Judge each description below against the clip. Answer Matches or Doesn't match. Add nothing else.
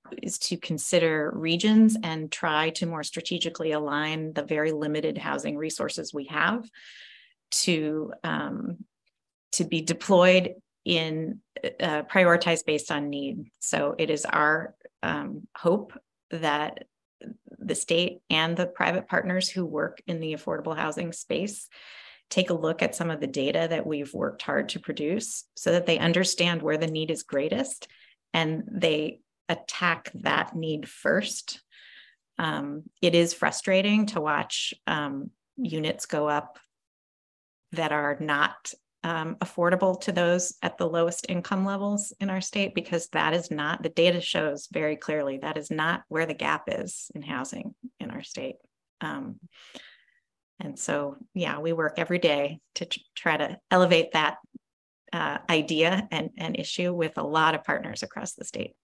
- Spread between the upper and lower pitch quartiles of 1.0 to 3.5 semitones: Matches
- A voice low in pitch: Doesn't match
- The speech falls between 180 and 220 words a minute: Doesn't match